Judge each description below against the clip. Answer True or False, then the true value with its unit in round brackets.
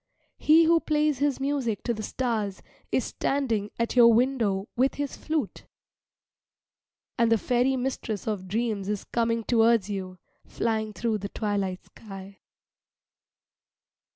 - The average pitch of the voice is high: True (230 Hz)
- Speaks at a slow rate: True (130 wpm)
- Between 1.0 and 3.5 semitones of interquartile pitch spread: False (4.2 semitones)